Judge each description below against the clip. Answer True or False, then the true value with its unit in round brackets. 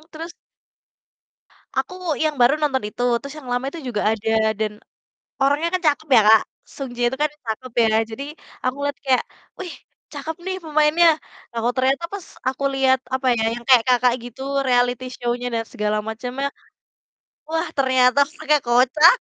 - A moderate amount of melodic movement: True (3.7 semitones)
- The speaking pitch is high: True (260 Hz)